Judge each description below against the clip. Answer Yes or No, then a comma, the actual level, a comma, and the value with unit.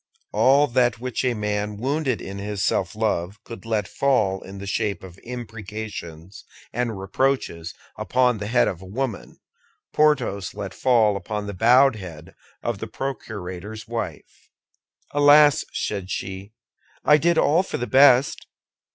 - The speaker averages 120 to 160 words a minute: Yes, average, 145 wpm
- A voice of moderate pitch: No, low, 110 Hz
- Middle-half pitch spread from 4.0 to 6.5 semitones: Yes, average, 4.5 semitones